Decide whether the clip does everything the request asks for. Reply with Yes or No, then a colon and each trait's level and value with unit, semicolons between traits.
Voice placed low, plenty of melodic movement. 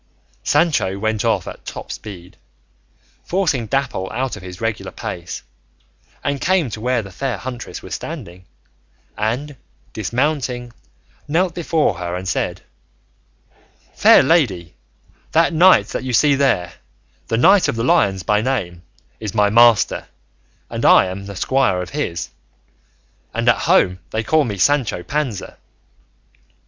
Yes: low, 115 Hz; wide, 6.8 semitones